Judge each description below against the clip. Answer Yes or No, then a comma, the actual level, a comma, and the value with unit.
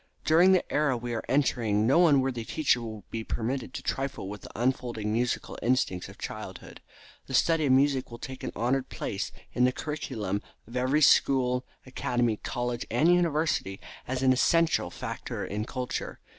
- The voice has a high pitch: No, low, 125 Hz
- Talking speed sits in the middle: Yes, average, 170 wpm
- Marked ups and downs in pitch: No, average, 3.0 semitones